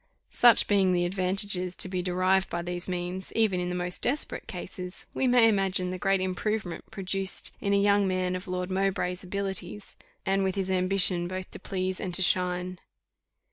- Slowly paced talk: No, average, 180 wpm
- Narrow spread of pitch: Yes, narrow, 1.3 semitones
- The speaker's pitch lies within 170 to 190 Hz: Yes, medium, 185 Hz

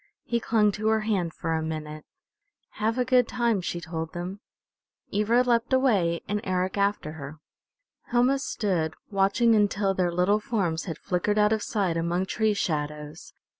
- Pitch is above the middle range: Yes, high, 200 Hz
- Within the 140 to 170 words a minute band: Yes, average, 165 wpm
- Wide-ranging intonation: No, average, 4.6 semitones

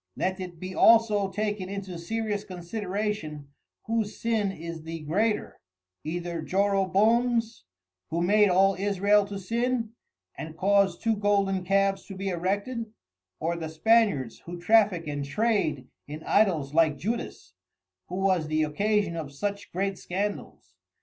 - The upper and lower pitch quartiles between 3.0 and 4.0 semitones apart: Yes, average, 3.7 semitones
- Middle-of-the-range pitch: No, high, 195 Hz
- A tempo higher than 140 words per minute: No, slow, 135 wpm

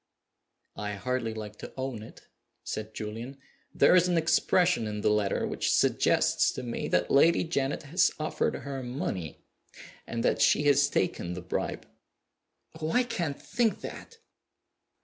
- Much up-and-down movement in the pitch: Yes, wide, 6.9 semitones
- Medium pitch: No, low, 130 Hz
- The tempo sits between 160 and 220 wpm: No, average, 150 wpm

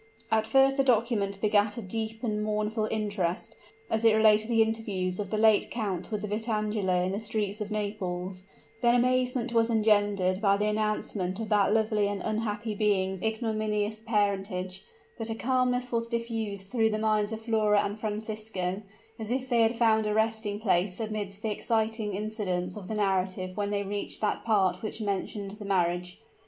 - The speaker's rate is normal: Yes, average, 175 wpm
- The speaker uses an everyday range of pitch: No, narrow, 1.9 semitones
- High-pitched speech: Yes, high, 215 Hz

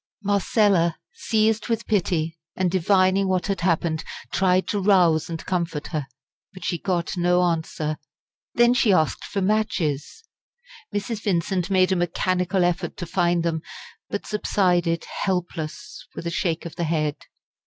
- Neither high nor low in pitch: Yes, medium, 180 Hz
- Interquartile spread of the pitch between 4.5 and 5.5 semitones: No, average, 2.8 semitones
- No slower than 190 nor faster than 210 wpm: No, average, 145 wpm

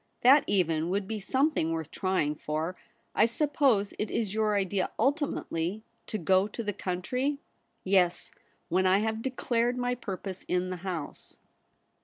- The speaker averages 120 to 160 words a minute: Yes, average, 155 wpm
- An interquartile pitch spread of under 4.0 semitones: No, average, 4.4 semitones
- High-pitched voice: Yes, high, 200 Hz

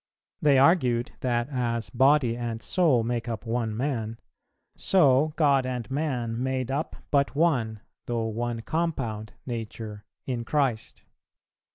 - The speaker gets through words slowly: Yes, slow, 130 wpm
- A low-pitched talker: Yes, low, 125 Hz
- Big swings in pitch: No, average, 3.3 semitones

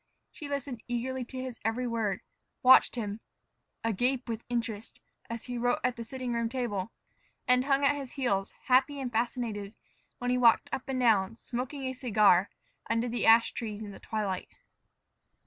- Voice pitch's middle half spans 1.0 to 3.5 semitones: Yes, narrow, 2.4 semitones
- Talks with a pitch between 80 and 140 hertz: No, high, 240 Hz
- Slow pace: No, average, 170 wpm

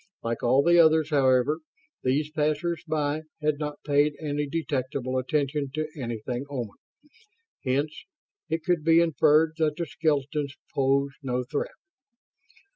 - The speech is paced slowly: Yes, slow, 130 wpm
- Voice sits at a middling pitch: Yes, medium, 145 Hz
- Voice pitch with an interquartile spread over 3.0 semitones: No, narrow, 2.6 semitones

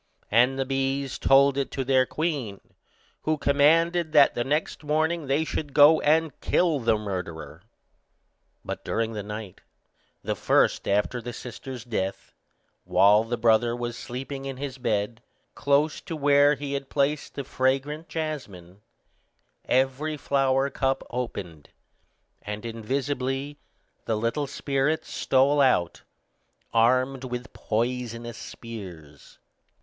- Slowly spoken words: Yes, slow, 125 wpm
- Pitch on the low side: Yes, low, 130 Hz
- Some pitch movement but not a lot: Yes, average, 3.8 semitones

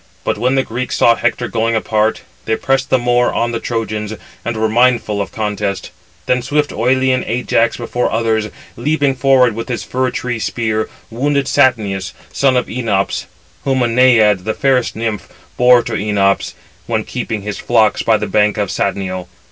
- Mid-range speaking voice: No, low, 115 Hz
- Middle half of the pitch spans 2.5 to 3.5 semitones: Yes, average, 2.9 semitones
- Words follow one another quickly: No, average, 170 wpm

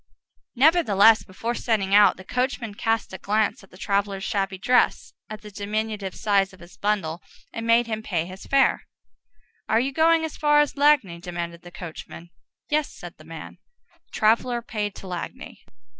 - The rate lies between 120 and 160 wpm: No, average, 175 wpm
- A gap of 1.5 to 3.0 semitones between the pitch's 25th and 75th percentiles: No, average, 4.0 semitones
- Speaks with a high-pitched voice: Yes, high, 210 Hz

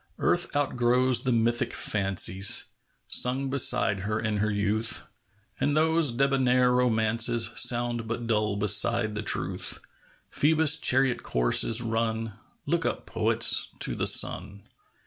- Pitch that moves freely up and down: No, average, 2.9 semitones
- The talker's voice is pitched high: No, low, 115 Hz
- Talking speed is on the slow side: Yes, slow, 125 wpm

